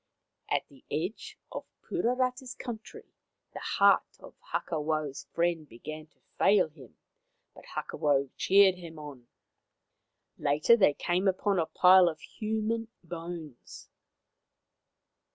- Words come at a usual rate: No, slow, 115 wpm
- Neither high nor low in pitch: Yes, medium, 170 Hz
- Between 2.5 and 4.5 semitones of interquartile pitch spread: No, average, 5.3 semitones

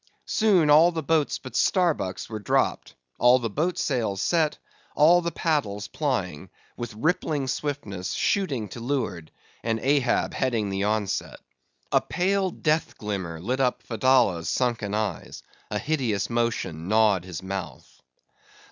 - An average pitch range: No, wide, 6.8 semitones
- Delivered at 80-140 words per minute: Yes, slow, 135 wpm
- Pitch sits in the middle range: No, low, 120 Hz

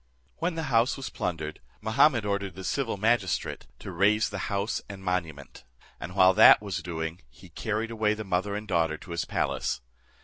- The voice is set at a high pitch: No, low, 100 Hz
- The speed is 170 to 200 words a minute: Yes, average, 180 wpm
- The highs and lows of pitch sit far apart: No, average, 3.6 semitones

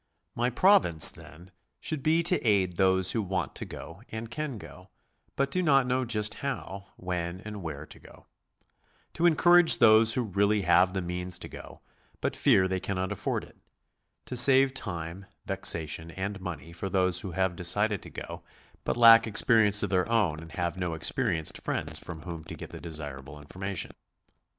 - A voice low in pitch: Yes, very low, 95 Hz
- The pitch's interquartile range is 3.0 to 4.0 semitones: No, average, 4.9 semitones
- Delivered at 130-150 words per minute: No, average, 180 wpm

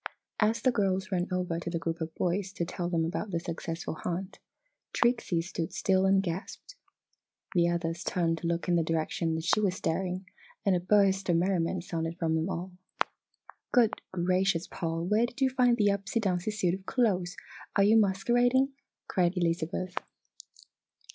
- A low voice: No, medium, 180 Hz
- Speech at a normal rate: Yes, average, 175 wpm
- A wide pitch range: No, average, 2.8 semitones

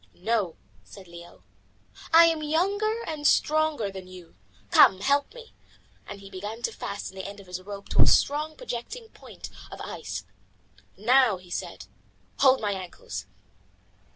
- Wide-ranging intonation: Yes, wide, 8.6 semitones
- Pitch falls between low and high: No, high, 220 Hz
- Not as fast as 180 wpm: Yes, average, 155 wpm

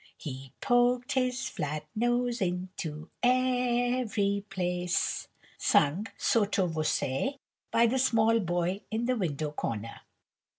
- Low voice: No, high, 205 Hz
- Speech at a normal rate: No, slow, 110 wpm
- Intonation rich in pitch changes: Yes, wide, 6.3 semitones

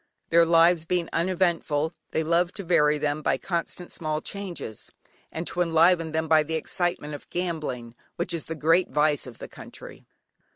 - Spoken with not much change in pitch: Yes, narrow, 2.3 semitones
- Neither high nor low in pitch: Yes, medium, 165 Hz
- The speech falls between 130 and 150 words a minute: No, average, 170 wpm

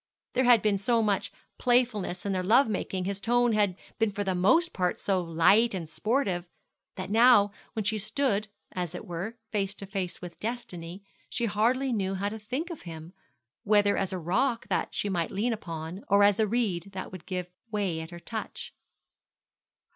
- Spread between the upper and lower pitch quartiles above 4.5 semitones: No, average, 3.7 semitones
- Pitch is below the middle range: No, high, 200 Hz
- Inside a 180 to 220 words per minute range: Yes, average, 190 wpm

